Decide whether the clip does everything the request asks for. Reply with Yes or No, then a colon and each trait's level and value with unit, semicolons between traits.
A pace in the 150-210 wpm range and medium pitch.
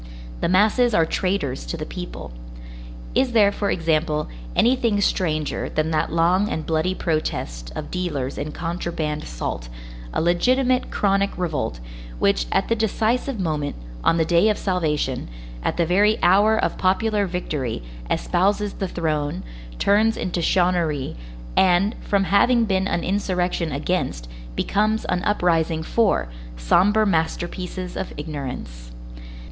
No: slow, 135 wpm; medium, 180 Hz